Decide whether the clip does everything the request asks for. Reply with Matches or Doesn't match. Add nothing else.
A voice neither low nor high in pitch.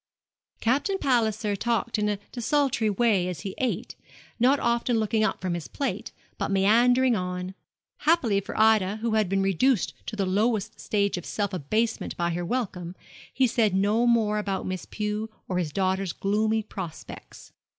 Doesn't match